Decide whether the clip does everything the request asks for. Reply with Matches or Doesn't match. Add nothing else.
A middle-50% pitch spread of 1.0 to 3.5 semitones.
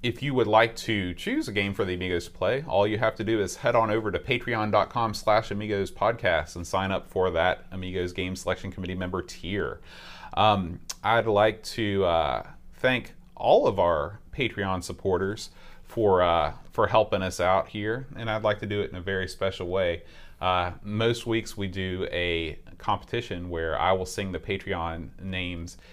Matches